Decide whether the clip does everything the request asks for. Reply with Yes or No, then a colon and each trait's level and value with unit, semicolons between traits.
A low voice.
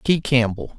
Yes: low, 125 Hz